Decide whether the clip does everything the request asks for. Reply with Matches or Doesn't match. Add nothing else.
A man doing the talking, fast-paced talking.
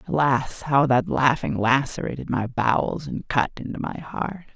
Doesn't match